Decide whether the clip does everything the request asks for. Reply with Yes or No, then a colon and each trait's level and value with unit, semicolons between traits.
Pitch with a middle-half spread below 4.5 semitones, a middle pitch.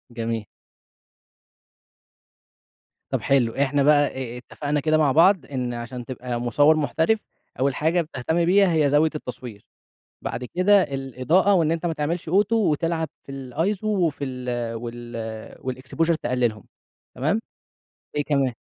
No: average, 4.8 semitones; medium, 145 Hz